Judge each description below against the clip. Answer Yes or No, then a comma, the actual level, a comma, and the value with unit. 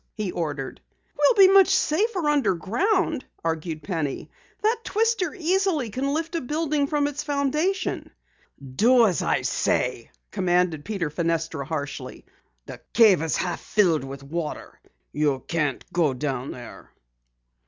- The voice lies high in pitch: Yes, high, 200 Hz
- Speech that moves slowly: Yes, slow, 130 wpm